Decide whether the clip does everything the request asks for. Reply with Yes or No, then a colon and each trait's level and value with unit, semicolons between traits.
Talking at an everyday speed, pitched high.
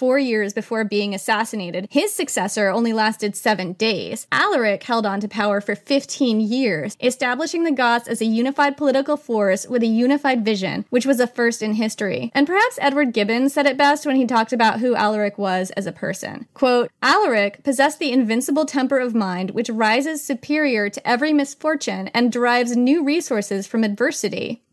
Yes: average, 180 wpm; high, 235 Hz